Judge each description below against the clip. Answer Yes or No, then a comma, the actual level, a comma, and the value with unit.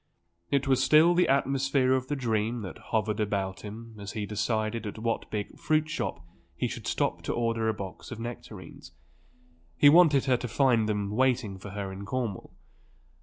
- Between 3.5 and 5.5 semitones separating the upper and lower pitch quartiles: Yes, average, 4.1 semitones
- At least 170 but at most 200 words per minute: Yes, average, 180 wpm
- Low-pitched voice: Yes, low, 115 Hz